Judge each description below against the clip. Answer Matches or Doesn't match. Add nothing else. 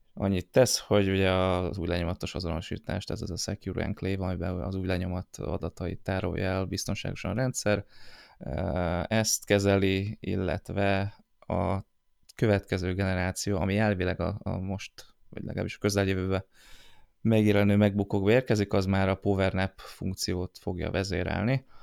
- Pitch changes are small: Matches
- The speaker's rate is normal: Matches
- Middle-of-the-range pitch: Doesn't match